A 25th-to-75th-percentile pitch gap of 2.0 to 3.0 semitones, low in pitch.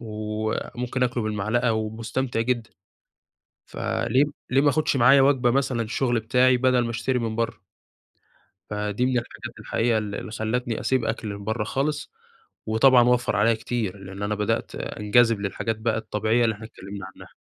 Yes: narrow, 2.6 semitones; low, 115 Hz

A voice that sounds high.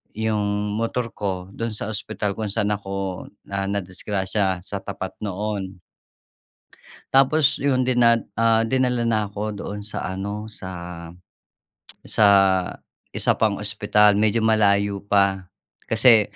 No: low, 105 Hz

